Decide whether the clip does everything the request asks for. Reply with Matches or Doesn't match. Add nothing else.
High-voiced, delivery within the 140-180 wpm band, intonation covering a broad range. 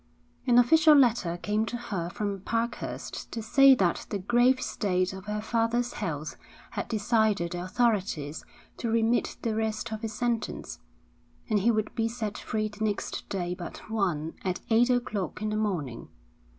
Doesn't match